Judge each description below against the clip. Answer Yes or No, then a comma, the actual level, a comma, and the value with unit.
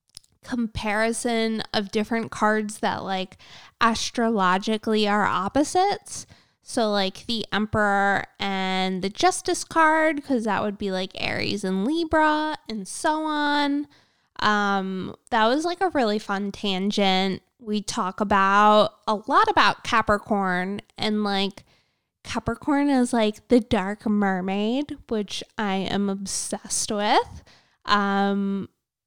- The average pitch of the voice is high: Yes, high, 215 Hz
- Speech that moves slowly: Yes, slow, 120 wpm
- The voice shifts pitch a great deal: No, average, 4.1 semitones